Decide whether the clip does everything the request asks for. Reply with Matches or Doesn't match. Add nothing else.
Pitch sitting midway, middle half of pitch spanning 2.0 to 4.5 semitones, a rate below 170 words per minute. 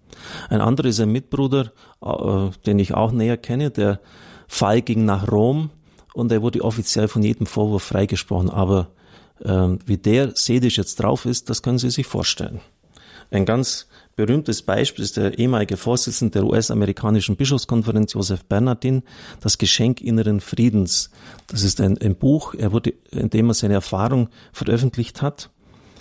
Doesn't match